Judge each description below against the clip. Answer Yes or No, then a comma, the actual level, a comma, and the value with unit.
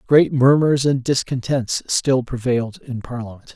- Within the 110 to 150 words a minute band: Yes, slow, 135 wpm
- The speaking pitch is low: Yes, low, 130 Hz